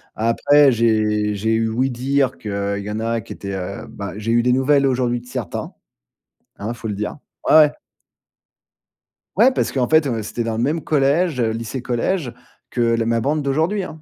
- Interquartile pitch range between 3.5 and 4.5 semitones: Yes, average, 3.9 semitones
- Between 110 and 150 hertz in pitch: Yes, low, 120 Hz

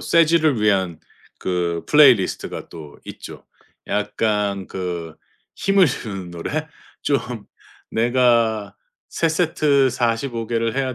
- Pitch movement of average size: No, wide, 6.4 semitones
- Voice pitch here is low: Yes, low, 115 Hz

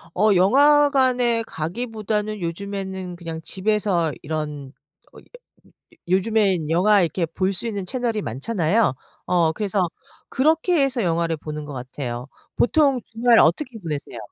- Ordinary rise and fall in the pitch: No, wide, 5.8 semitones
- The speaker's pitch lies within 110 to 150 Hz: No, high, 190 Hz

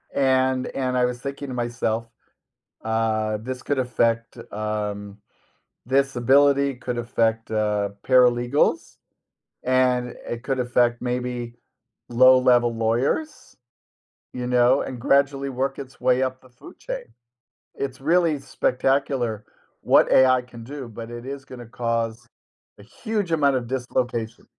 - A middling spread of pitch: No, narrow, 2.2 semitones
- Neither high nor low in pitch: No, low, 125 Hz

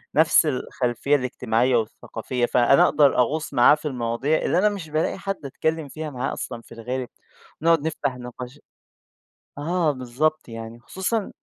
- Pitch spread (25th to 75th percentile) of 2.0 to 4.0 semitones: No, average, 4.4 semitones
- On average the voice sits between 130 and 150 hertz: Yes, low, 135 Hz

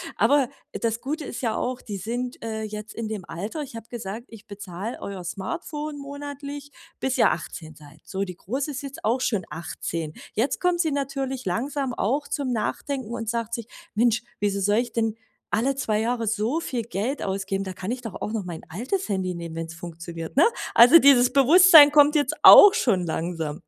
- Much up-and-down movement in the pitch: Yes, wide, 5.9 semitones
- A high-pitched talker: Yes, high, 230 Hz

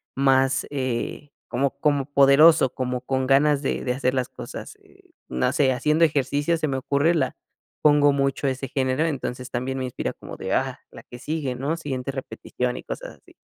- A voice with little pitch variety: Yes, narrow, 2.1 semitones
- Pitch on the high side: No, low, 135 Hz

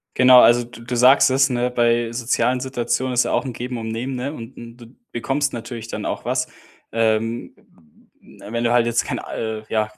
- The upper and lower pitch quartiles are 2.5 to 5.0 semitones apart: No, narrow, 1.6 semitones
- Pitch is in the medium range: No, low, 120 Hz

